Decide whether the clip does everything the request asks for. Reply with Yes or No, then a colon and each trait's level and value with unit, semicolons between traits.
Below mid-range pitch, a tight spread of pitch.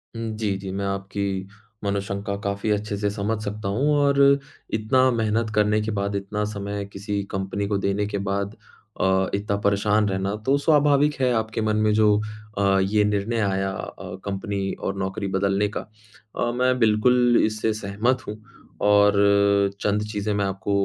Yes: low, 105 Hz; narrow, 1.7 semitones